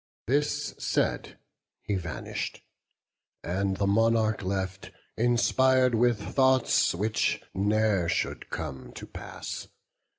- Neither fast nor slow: No, slow, 100 wpm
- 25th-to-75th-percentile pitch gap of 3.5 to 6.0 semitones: Yes, average, 4.2 semitones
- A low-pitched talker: Yes, low, 110 Hz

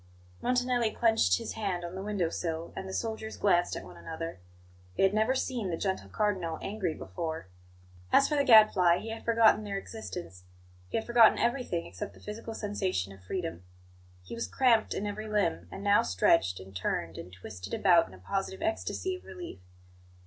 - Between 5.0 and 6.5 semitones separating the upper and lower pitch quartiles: Yes, average, 5.3 semitones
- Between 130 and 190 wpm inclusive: Yes, average, 185 wpm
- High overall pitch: Yes, high, 195 Hz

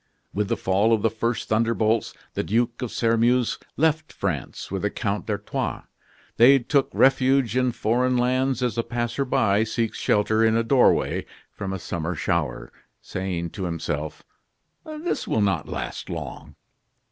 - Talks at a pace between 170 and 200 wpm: No, average, 160 wpm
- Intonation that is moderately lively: Yes, average, 3.7 semitones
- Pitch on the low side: Yes, low, 115 Hz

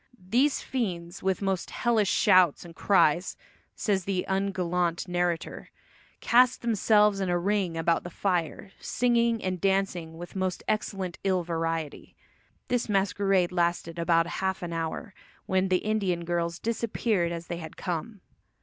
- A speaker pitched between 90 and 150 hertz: No, medium, 185 Hz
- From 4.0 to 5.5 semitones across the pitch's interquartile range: No, average, 2.9 semitones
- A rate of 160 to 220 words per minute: No, average, 140 wpm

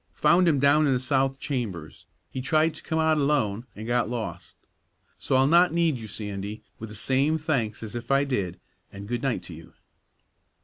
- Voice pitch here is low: Yes, low, 130 Hz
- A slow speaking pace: No, average, 195 wpm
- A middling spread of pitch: No, wide, 5.7 semitones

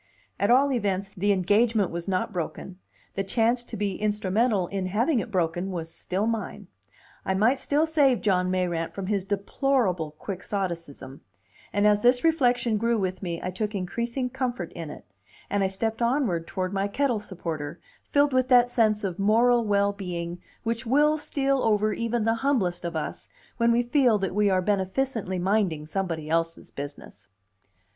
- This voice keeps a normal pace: Yes, average, 170 wpm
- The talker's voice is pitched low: No, high, 205 Hz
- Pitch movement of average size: Yes, average, 4.5 semitones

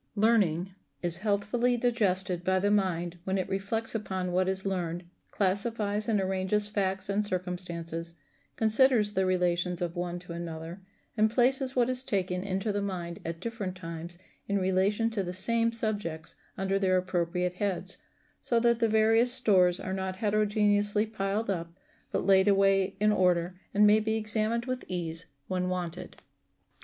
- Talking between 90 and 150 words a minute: No, average, 160 wpm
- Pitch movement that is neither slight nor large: Yes, average, 3.0 semitones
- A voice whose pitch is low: No, high, 195 Hz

